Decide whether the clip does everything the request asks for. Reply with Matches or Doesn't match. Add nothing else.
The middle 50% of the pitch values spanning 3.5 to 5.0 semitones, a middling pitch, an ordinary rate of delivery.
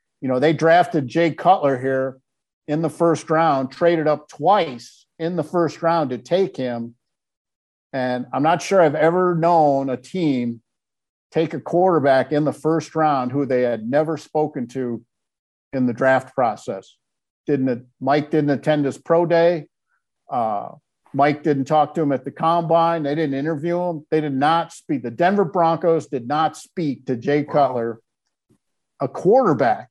Matches